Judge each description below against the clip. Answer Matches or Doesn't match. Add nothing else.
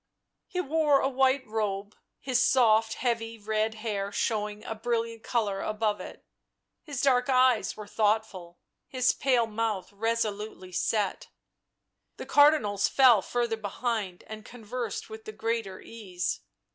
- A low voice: Doesn't match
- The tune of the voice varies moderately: Matches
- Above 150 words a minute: Doesn't match